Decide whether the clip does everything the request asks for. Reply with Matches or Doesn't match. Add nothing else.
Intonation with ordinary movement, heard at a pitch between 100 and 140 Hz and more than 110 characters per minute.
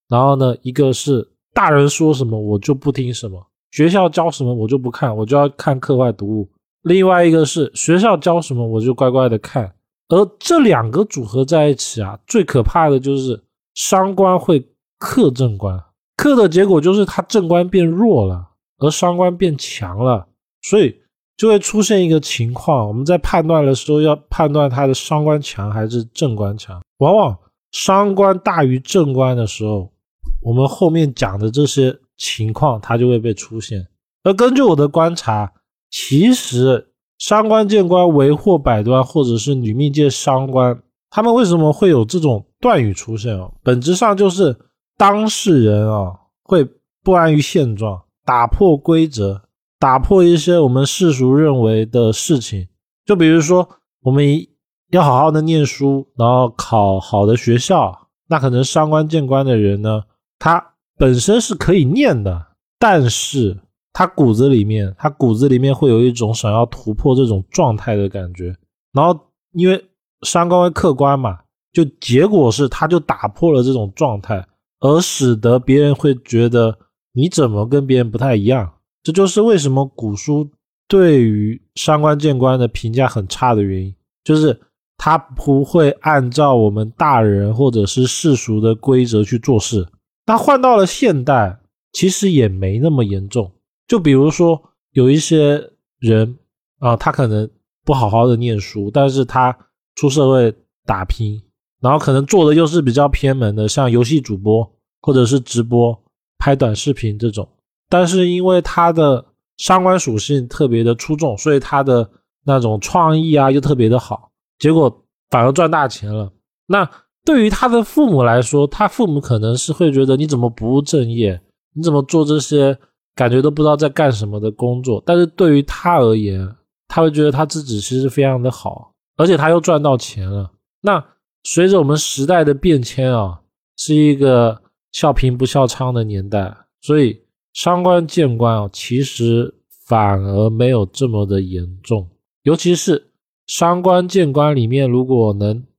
Doesn't match